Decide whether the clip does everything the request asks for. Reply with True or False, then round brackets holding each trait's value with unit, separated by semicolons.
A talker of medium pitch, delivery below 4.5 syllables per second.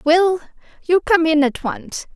False (325 Hz; 4.1 syllables/s)